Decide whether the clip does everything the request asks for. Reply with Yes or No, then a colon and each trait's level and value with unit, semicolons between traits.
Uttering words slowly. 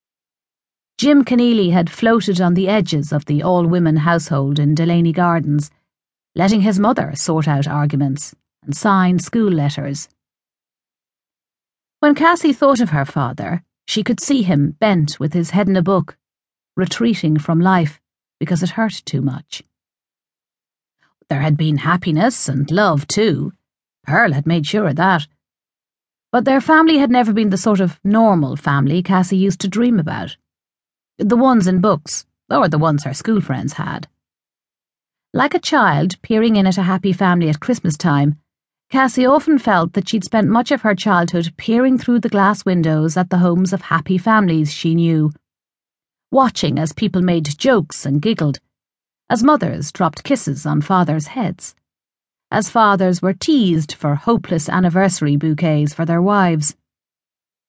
No: average, 155 wpm